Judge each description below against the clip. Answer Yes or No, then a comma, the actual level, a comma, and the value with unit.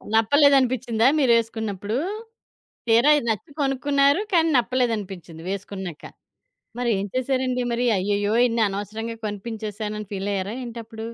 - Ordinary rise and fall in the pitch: Yes, average, 3.7 semitones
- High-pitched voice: Yes, high, 225 Hz